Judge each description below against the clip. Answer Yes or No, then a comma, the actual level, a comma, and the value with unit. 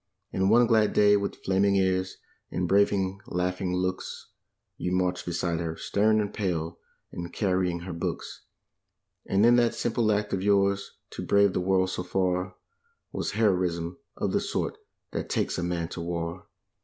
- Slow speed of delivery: No, average, 165 wpm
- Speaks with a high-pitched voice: No, very low, 95 Hz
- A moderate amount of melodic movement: No, narrow, 2.1 semitones